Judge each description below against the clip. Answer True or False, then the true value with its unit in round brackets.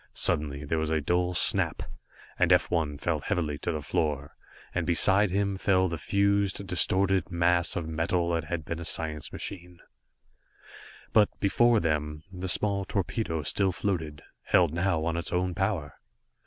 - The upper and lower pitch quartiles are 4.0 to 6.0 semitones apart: False (3.4 semitones)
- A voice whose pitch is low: True (85 Hz)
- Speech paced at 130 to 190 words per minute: True (160 wpm)